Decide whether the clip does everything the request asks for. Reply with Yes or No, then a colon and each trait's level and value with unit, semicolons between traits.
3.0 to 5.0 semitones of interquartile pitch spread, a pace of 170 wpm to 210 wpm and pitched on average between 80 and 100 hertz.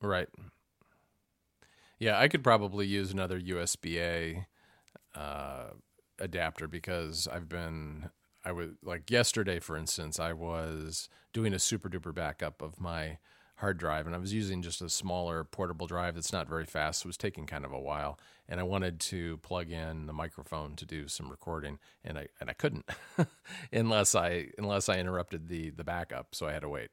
No: narrow, 2.5 semitones; average, 185 wpm; very low, 85 Hz